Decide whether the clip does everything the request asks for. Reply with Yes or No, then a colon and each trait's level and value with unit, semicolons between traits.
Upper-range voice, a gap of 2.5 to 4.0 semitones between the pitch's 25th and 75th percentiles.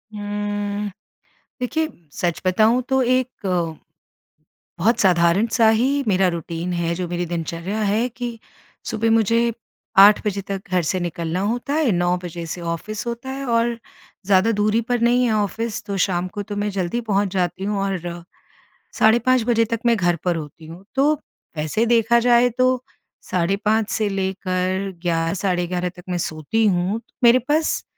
No: high, 205 Hz; average, 4.6 semitones